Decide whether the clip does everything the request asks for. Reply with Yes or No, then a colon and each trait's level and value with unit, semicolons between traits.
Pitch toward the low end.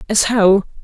No: high, 200 Hz